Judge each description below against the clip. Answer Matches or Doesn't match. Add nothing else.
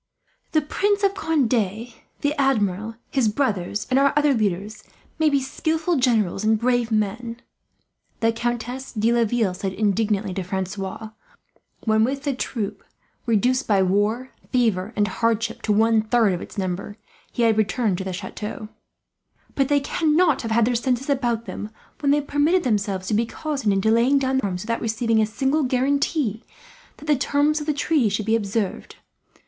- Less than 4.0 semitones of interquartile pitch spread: Doesn't match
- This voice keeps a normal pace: Matches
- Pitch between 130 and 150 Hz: Doesn't match